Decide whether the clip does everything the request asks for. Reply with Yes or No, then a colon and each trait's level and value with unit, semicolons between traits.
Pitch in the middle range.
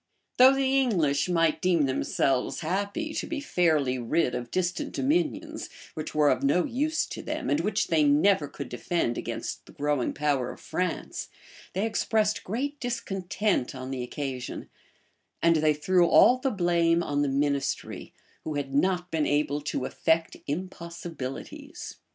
Yes: medium, 170 Hz